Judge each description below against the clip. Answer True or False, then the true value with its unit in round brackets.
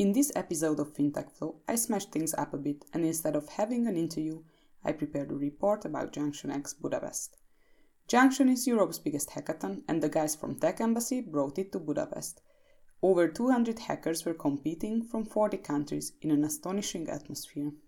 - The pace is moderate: True (175 wpm)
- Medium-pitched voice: True (165 Hz)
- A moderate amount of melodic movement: False (7.3 semitones)